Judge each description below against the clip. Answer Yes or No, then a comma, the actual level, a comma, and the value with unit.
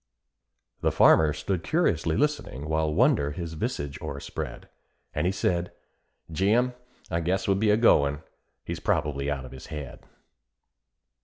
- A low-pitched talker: Yes, very low, 80 Hz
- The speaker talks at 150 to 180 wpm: No, average, 140 wpm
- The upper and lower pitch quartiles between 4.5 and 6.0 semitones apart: Yes, wide, 5.4 semitones